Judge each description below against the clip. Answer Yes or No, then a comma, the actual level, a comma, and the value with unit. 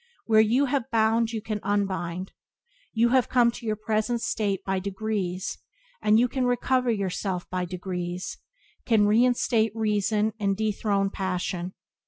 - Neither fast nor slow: Yes, average, 145 wpm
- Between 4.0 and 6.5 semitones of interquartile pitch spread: No, average, 3.1 semitones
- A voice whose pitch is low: No, high, 215 Hz